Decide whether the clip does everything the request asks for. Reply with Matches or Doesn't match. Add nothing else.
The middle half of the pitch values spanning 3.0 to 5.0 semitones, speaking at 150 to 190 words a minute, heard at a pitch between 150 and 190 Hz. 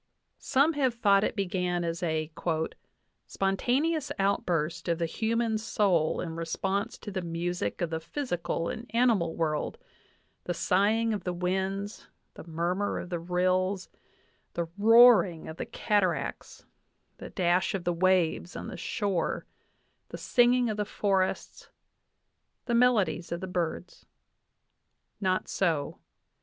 Doesn't match